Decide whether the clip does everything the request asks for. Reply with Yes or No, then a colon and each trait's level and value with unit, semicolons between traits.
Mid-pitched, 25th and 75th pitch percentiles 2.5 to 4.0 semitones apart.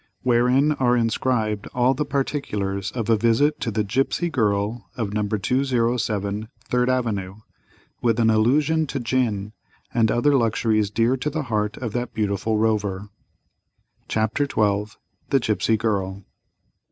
No: low, 115 Hz; average, 3.4 semitones